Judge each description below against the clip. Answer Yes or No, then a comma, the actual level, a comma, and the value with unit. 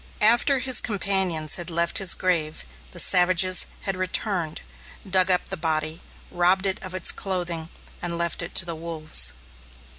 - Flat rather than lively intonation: Yes, narrow, 2.3 semitones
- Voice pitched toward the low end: No, medium, 180 Hz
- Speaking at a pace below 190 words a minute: Yes, average, 155 wpm